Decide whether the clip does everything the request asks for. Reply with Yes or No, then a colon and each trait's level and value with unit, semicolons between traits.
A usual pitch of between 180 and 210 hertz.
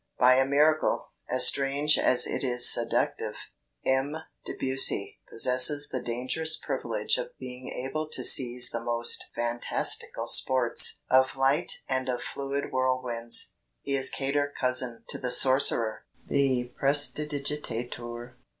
No: low, 130 Hz